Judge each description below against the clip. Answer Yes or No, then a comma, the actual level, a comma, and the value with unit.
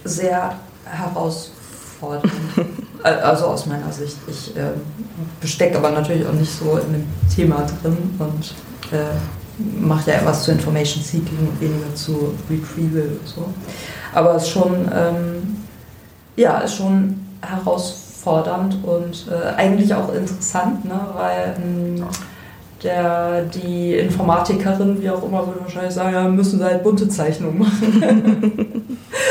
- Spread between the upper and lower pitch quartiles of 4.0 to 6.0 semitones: No, average, 3.5 semitones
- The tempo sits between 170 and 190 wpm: No, average, 130 wpm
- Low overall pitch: No, medium, 175 Hz